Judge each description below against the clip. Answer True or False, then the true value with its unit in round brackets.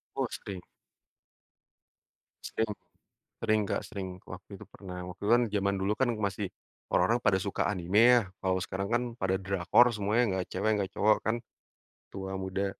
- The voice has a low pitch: True (100 Hz)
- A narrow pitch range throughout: True (2.3 semitones)